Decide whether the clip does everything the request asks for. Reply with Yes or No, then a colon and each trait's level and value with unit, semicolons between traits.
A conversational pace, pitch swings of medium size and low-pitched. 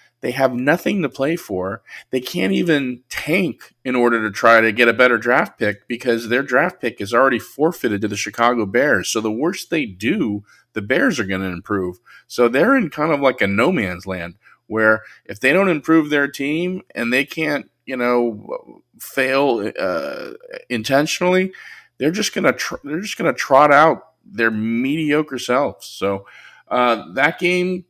No: average, 185 wpm; wide, 5.7 semitones; low, 125 Hz